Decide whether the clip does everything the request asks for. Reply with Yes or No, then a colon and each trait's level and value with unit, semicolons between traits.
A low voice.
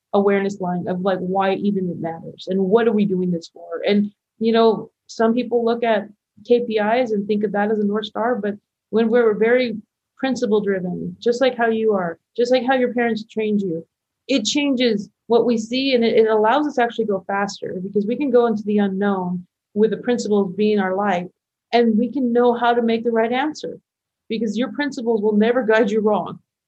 No: high, 220 Hz